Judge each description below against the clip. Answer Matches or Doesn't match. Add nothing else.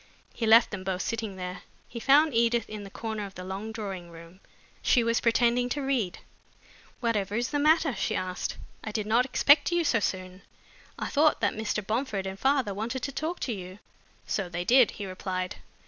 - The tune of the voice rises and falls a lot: Doesn't match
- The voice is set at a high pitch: Matches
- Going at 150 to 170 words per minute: Doesn't match